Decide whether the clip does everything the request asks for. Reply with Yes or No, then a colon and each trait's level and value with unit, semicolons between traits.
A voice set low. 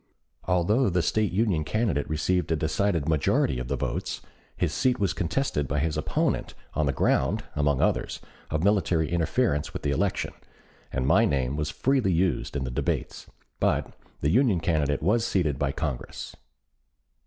Yes: very low, 80 Hz